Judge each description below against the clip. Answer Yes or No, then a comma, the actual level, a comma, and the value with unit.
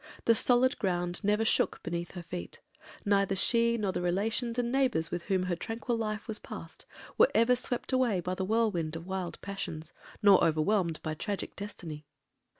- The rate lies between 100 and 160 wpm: No, average, 175 wpm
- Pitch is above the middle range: Yes, high, 200 Hz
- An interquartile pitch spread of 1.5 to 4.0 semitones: No, average, 4.7 semitones